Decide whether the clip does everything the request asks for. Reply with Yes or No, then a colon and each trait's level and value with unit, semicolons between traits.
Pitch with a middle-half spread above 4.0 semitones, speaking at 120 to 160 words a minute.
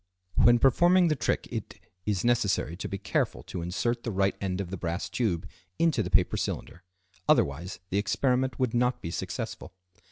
No: wide, 5.4 semitones; average, 180 wpm